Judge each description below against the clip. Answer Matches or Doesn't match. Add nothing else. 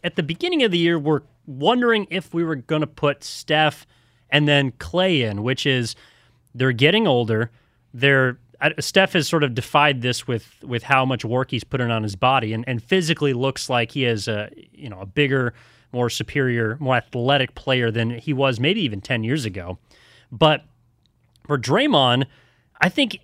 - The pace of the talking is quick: Doesn't match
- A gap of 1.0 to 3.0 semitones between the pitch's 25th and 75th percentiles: Doesn't match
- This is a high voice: Doesn't match